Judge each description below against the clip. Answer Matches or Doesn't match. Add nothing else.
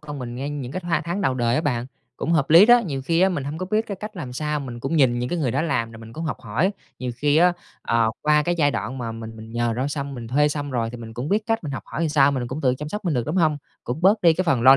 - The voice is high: Doesn't match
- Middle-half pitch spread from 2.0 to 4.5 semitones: Doesn't match